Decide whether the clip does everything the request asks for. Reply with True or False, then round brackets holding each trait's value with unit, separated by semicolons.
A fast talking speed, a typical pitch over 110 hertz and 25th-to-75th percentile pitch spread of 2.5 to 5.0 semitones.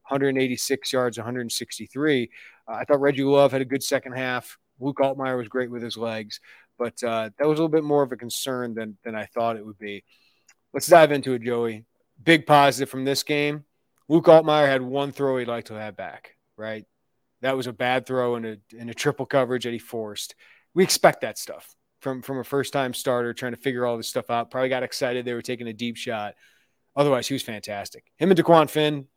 True (220 wpm; 130 Hz; 2.9 semitones)